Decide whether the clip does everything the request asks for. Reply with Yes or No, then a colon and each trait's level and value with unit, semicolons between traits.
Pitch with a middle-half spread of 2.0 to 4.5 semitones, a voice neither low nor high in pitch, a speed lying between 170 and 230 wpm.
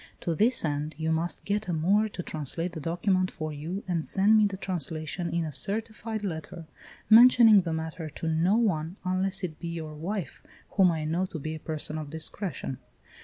Yes: average, 3.8 semitones; medium, 170 Hz; average, 195 wpm